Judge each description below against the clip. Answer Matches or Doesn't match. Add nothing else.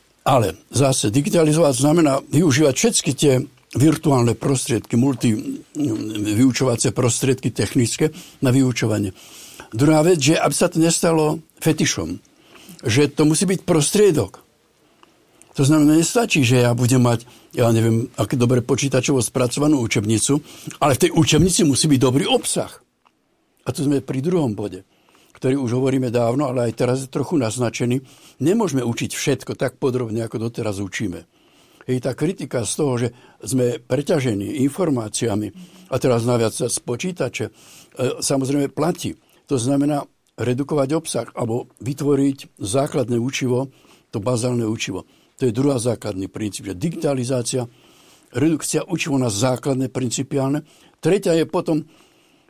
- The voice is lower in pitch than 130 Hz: Doesn't match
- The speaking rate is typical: Matches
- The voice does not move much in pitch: Doesn't match